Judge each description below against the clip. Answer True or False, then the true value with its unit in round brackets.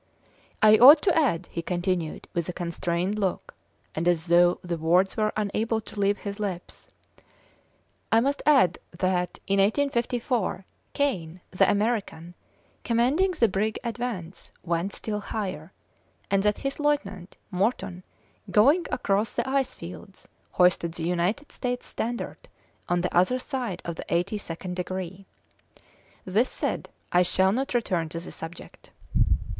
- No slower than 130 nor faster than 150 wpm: True (140 wpm)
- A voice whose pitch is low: False (195 Hz)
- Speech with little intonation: False (5.0 semitones)